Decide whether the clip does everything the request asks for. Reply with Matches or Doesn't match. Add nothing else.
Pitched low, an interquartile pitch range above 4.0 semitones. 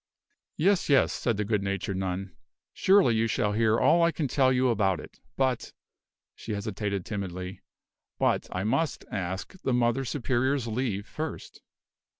Matches